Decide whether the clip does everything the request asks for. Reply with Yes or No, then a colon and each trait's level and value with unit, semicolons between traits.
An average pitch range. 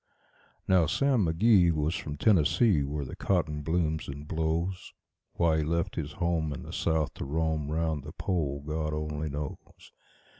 No: narrow, 2.2 semitones